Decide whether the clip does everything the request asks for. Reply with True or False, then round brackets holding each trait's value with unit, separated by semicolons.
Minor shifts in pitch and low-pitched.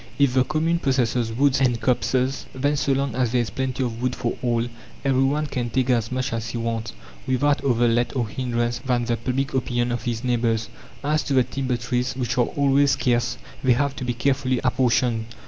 True (2.1 semitones; 125 Hz)